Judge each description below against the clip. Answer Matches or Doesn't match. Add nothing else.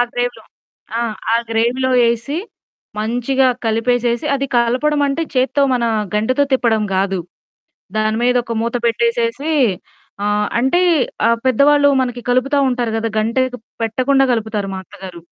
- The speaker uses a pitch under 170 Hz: Doesn't match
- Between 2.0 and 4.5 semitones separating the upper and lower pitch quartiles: Matches